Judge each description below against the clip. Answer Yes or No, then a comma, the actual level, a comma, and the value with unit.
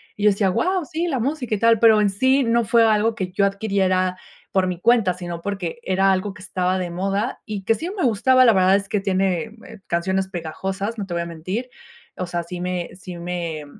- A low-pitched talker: No, high, 195 Hz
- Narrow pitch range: No, average, 3.7 semitones